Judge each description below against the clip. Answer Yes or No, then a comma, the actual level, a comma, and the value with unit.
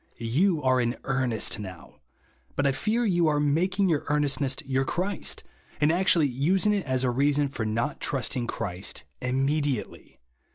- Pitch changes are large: No, average, 4.6 semitones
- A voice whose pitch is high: No, medium, 140 Hz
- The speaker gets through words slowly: No, average, 155 wpm